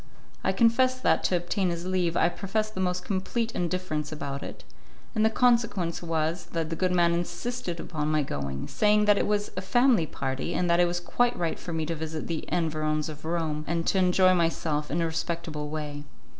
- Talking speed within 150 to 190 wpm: No, fast, 205 wpm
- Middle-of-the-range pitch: Yes, medium, 170 Hz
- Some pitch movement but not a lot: Yes, average, 3.3 semitones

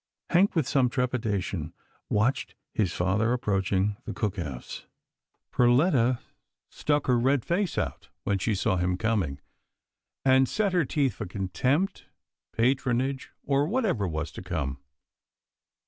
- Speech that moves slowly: Yes, slow, 130 wpm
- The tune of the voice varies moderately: No, wide, 6.3 semitones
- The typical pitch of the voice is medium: No, low, 120 Hz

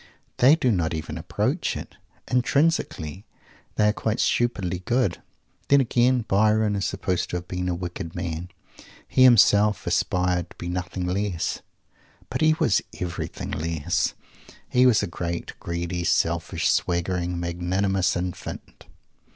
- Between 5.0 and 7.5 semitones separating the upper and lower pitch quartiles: No, average, 3.9 semitones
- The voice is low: Yes, very low, 90 Hz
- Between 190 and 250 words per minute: No, slow, 135 wpm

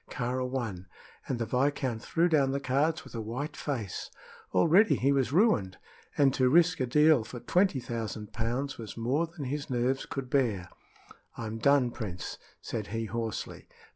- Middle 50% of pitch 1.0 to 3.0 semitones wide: No, average, 4.0 semitones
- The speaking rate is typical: Yes, average, 170 wpm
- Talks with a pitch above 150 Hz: No, low, 130 Hz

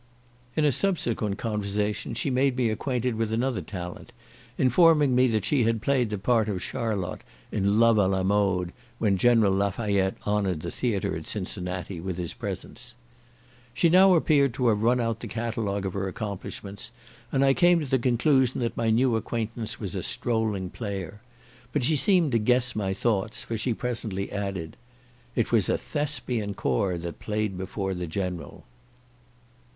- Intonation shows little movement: No, average, 4.1 semitones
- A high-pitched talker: No, low, 110 Hz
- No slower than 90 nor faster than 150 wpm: No, average, 170 wpm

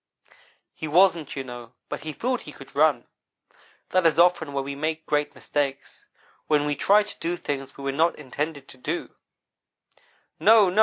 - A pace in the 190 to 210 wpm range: No, average, 175 wpm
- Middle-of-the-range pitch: Yes, medium, 150 Hz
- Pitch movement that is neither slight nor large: Yes, average, 3.5 semitones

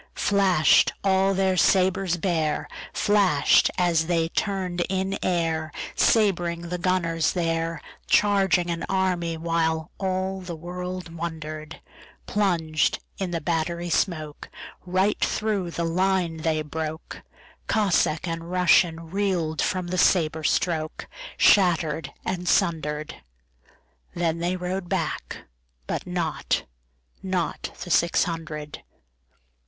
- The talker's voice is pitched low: No, medium, 170 Hz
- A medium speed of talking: No, slow, 90 wpm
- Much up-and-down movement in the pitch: No, narrow, 2.5 semitones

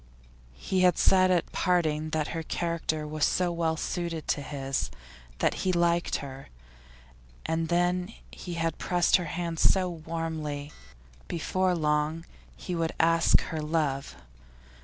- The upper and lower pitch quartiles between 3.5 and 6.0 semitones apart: No, narrow, 2.4 semitones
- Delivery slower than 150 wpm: Yes, average, 140 wpm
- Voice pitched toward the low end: No, medium, 165 Hz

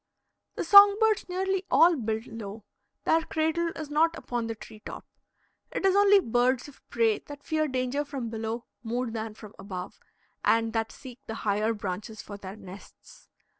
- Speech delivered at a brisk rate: No, average, 170 wpm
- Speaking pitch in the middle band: No, high, 240 Hz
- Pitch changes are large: Yes, wide, 6.3 semitones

